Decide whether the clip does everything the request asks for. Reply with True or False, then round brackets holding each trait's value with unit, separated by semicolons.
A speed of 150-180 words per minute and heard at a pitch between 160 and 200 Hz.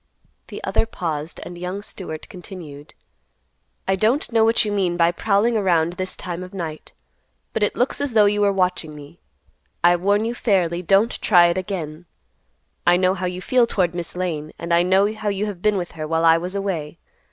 False (200 wpm; 185 Hz)